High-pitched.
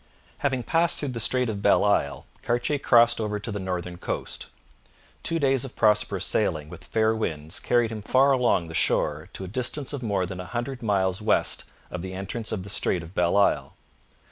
No: low, 105 Hz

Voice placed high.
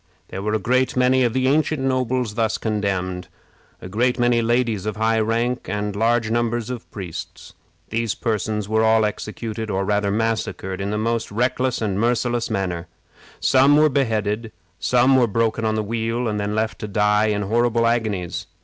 No: low, 110 Hz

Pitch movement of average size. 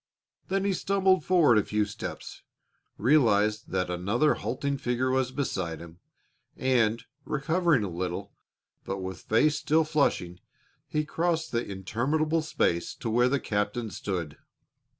No: wide, 7.4 semitones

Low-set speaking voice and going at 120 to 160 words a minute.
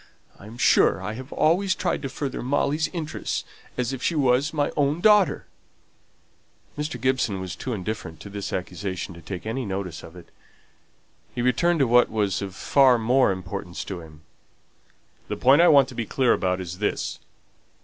No: low, 120 Hz; average, 180 wpm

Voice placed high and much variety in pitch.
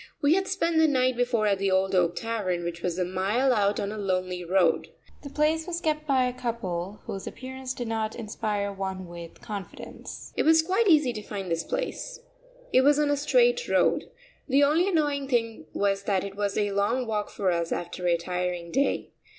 Yes: high, 215 Hz; wide, 7.1 semitones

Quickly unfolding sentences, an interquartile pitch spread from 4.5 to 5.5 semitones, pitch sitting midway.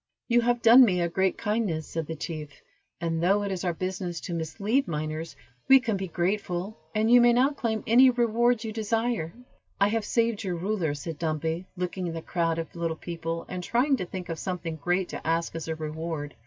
Yes: fast, 210 wpm; average, 5.1 semitones; medium, 180 Hz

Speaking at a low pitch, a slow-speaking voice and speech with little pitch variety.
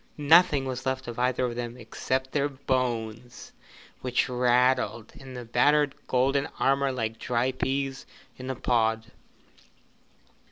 Yes: low, 130 Hz; slow, 130 wpm; narrow, 1.9 semitones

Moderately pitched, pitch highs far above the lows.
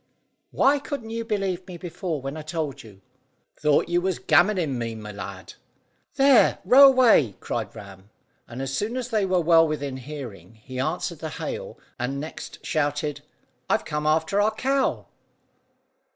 Yes: medium, 155 Hz; wide, 7.3 semitones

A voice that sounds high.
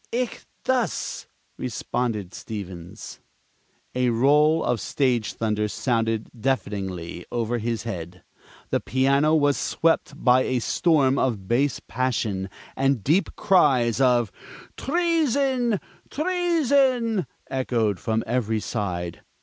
No: low, 125 Hz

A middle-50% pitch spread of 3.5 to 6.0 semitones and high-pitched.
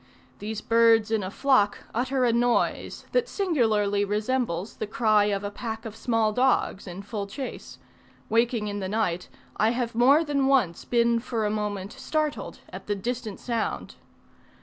No: average, 3.1 semitones; high, 225 Hz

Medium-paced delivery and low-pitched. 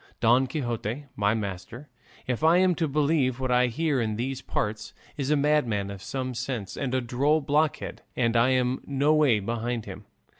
Yes: average, 185 wpm; low, 130 Hz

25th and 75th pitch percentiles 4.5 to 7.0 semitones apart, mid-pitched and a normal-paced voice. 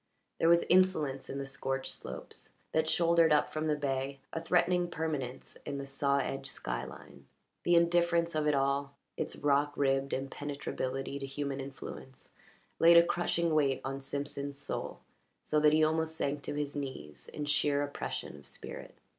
No: average, 2.8 semitones; medium, 145 Hz; average, 170 wpm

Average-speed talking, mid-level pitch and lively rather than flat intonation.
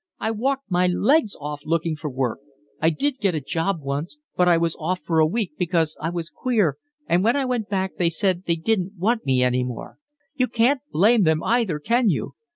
No: fast, 215 wpm; medium, 180 Hz; wide, 6.0 semitones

